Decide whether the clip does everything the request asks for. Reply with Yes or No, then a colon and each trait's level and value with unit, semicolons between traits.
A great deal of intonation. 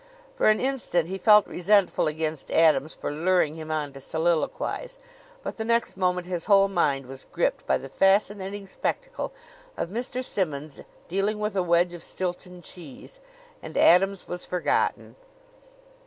No: average, 4.0 semitones